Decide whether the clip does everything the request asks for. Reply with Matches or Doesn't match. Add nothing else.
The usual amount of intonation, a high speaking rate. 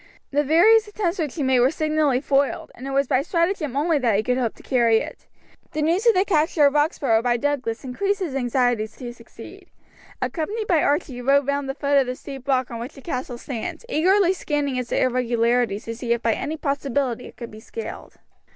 Matches